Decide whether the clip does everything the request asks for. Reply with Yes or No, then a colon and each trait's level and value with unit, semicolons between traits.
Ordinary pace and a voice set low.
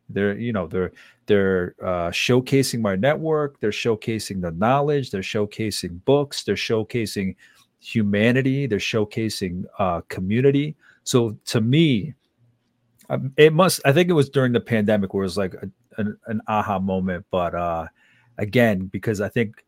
Yes: average, 150 wpm; low, 110 Hz